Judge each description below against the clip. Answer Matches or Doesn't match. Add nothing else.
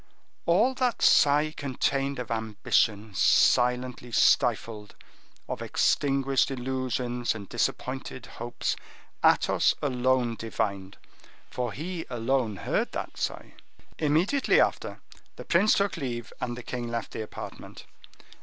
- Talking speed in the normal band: Doesn't match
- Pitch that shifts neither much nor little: Matches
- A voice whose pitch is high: Doesn't match